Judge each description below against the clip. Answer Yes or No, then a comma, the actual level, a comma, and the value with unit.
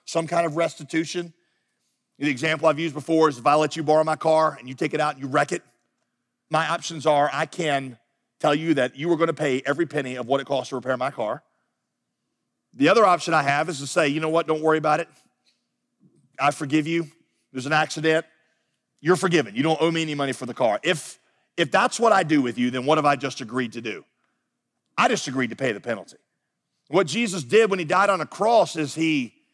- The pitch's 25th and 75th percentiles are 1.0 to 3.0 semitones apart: Yes, narrow, 2.6 semitones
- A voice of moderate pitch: Yes, medium, 155 Hz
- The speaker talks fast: Yes, fast, 235 wpm